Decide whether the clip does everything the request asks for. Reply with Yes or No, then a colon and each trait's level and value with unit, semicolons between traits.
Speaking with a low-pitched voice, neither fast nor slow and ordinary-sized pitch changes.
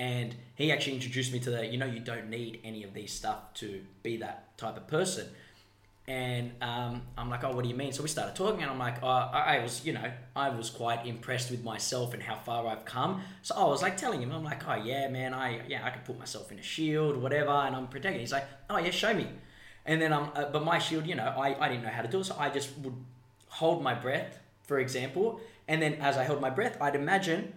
No: low, 130 Hz; fast, 260 wpm; average, 3.3 semitones